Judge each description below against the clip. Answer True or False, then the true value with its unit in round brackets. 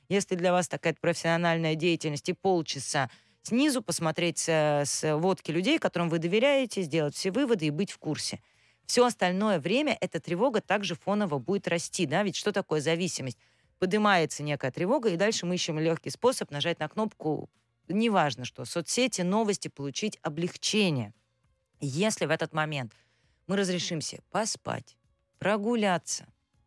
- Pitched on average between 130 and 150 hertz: False (170 Hz)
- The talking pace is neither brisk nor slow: True (140 wpm)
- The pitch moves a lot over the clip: False (4.6 semitones)